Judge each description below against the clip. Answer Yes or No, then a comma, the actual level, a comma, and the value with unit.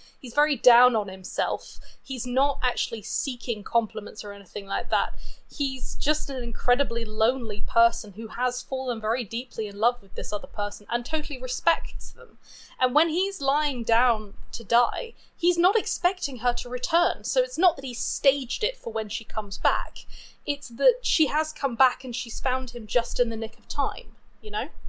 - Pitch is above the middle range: Yes, very high, 250 Hz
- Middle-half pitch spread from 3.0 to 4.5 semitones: Yes, average, 3.8 semitones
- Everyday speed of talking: Yes, average, 190 wpm